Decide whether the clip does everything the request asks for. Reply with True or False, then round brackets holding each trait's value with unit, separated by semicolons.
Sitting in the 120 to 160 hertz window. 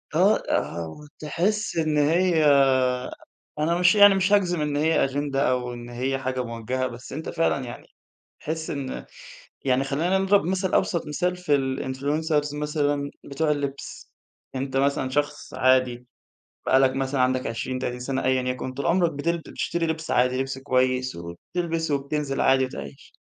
True (140 Hz)